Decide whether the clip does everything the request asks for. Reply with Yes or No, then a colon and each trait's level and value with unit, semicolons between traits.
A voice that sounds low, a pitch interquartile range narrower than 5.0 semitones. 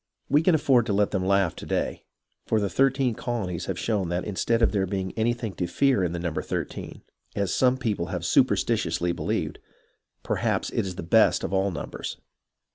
Yes: low, 100 Hz; average, 4.5 semitones